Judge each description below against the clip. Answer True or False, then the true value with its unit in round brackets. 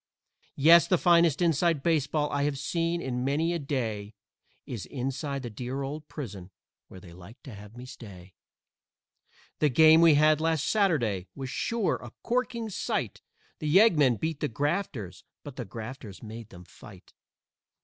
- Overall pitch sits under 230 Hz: True (140 Hz)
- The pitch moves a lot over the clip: True (5.8 semitones)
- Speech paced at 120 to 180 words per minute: True (160 wpm)